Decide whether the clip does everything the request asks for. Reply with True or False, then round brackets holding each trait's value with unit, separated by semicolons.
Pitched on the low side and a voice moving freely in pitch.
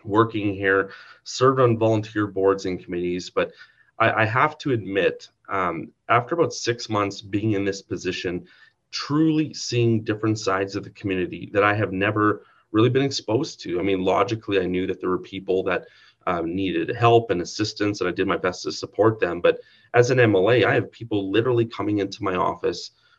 False (105 Hz; 3.4 semitones)